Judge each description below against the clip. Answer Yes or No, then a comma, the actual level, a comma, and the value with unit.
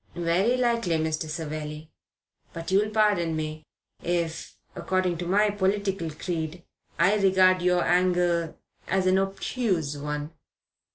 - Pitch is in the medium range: Yes, medium, 175 Hz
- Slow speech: Yes, slow, 120 wpm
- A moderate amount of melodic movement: Yes, average, 3.2 semitones